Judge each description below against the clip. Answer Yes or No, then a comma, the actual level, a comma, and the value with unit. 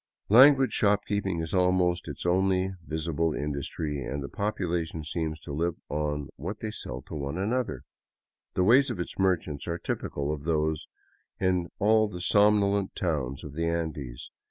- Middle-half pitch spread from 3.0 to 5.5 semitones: Yes, average, 4.6 semitones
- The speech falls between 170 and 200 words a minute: No, average, 155 wpm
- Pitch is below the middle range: Yes, very low, 85 Hz